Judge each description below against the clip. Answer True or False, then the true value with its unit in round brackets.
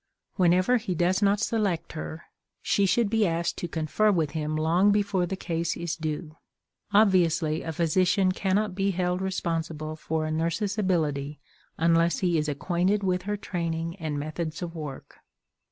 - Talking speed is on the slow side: False (160 wpm)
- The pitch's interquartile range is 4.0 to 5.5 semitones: False (3.1 semitones)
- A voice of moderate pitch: True (170 Hz)